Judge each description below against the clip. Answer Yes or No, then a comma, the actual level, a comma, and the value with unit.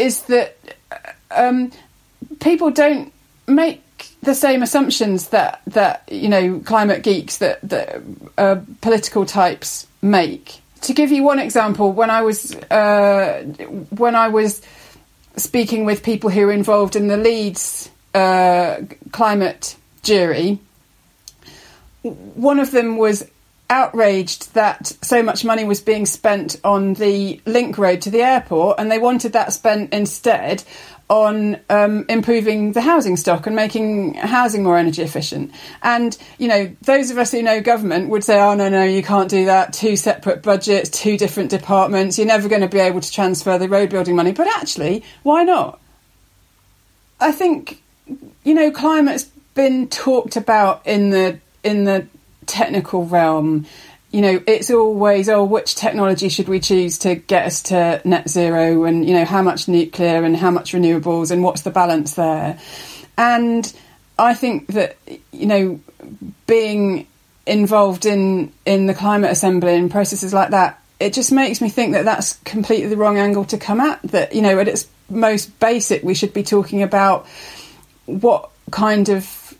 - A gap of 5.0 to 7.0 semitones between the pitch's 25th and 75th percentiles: No, average, 3.5 semitones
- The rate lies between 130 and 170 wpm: Yes, average, 160 wpm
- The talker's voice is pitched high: Yes, high, 205 Hz